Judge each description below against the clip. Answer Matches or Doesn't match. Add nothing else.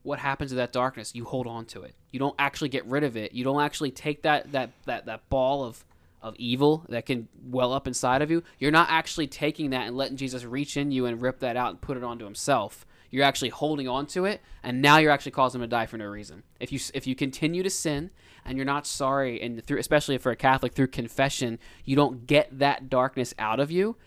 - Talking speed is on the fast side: Matches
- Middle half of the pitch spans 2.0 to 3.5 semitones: Matches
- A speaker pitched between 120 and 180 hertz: Matches